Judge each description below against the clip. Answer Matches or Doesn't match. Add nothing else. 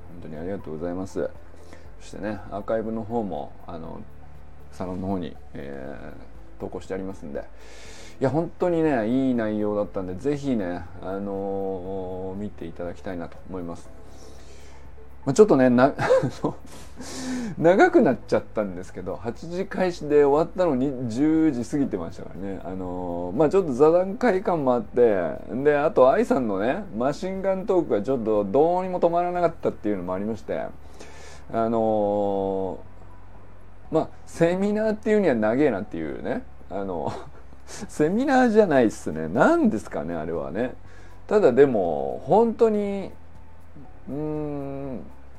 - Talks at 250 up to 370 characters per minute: Matches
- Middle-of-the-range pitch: Doesn't match